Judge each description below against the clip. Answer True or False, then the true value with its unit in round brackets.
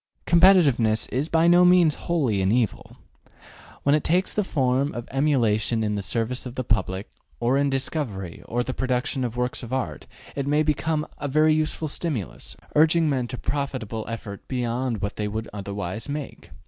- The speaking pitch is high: False (130 Hz)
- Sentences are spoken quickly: False (175 wpm)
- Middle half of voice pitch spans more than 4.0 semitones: True (5.3 semitones)